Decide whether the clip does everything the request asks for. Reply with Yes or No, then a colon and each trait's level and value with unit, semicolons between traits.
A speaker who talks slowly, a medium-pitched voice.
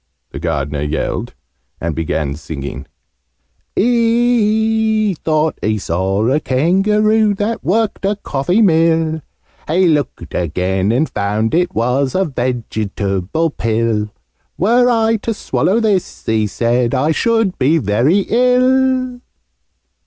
Yes: slow, 115 wpm; medium, 160 Hz